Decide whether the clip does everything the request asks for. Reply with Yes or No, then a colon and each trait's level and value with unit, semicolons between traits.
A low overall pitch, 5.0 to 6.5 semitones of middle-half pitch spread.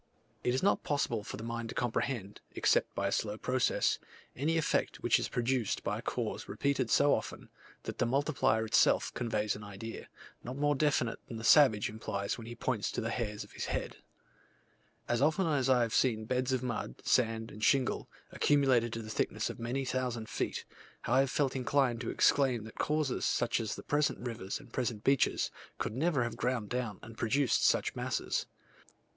No: low, 120 Hz; average, 3.2 semitones